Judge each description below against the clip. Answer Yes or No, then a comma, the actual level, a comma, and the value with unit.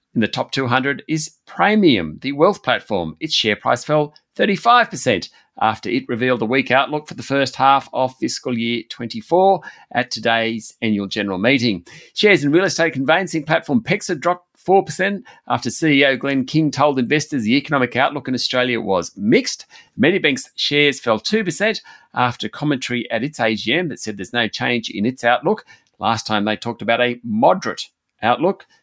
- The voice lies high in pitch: No, low, 135 Hz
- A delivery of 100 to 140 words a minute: No, average, 165 wpm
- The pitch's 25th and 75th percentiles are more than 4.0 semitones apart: Yes, wide, 5.6 semitones